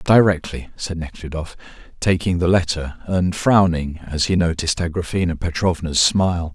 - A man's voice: Yes, male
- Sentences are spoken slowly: Yes, slow, 130 wpm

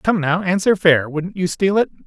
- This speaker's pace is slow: No, fast, 205 wpm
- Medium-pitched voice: Yes, medium, 180 Hz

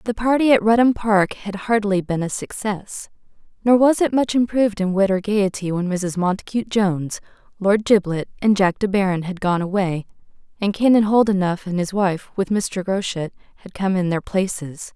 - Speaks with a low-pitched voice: No, high, 200 Hz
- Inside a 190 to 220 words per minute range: No, average, 180 wpm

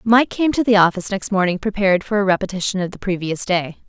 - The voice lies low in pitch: No, high, 195 Hz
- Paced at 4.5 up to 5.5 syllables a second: No, 6.5 syllables/s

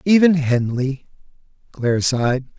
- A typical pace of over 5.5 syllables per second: No, 4.6 syllables/s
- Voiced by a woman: No, male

